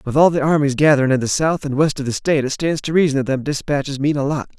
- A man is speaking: Yes, male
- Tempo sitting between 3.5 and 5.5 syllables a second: No, 6.8 syllables/s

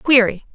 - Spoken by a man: No, female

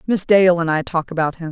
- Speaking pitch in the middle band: Yes, medium, 175 Hz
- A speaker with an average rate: No, fast, 280 wpm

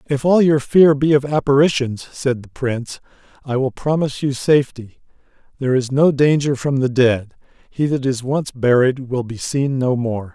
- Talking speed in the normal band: Yes, average, 185 wpm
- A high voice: No, low, 135 Hz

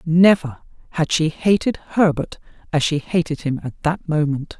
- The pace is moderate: Yes, average, 155 wpm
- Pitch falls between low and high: Yes, medium, 160 Hz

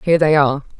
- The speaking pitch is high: No, medium, 150 Hz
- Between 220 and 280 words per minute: Yes, fast, 230 wpm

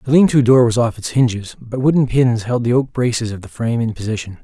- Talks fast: Yes, fast, 270 wpm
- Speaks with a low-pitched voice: Yes, low, 120 Hz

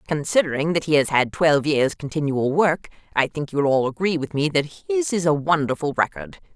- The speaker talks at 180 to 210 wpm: Yes, average, 200 wpm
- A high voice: No, medium, 155 Hz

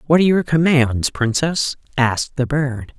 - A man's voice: No, female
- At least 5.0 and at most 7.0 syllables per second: No, 4.6 syllables/s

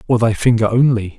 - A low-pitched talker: Yes, low, 115 Hz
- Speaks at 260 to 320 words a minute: No, fast, 205 wpm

